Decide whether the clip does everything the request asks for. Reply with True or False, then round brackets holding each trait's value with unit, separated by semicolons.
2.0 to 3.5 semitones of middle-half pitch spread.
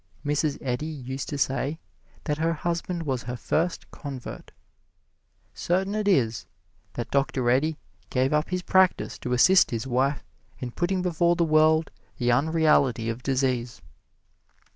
False (4.7 semitones)